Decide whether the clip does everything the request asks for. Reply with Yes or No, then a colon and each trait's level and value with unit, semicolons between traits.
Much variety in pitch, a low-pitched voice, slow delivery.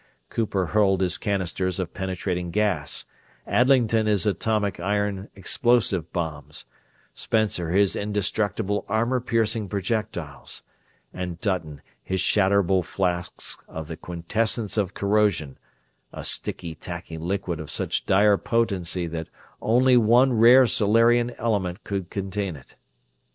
No: average, 3.6 semitones; low, 100 Hz; slow, 120 wpm